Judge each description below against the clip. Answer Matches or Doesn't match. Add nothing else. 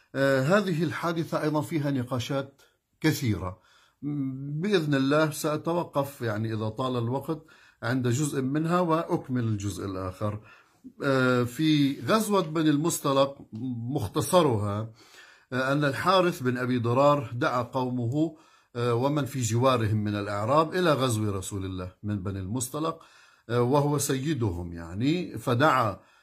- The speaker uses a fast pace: Doesn't match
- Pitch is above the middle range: Doesn't match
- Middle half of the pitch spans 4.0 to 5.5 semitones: Matches